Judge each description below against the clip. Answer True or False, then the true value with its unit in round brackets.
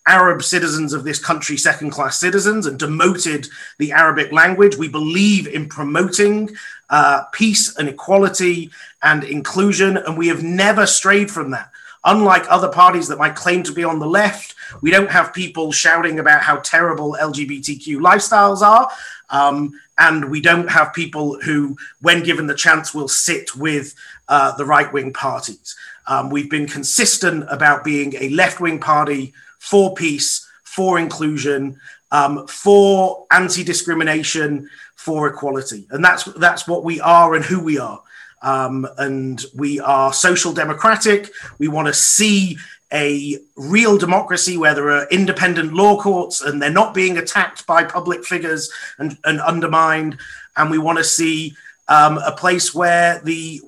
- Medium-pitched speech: True (165 Hz)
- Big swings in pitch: False (3.7 semitones)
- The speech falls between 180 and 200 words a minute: False (155 wpm)